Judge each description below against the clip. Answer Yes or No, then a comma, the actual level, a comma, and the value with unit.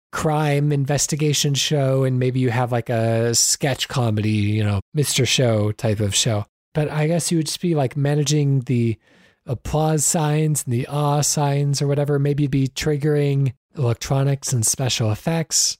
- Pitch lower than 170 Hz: Yes, medium, 140 Hz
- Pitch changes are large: No, average, 3.6 semitones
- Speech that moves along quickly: No, average, 165 wpm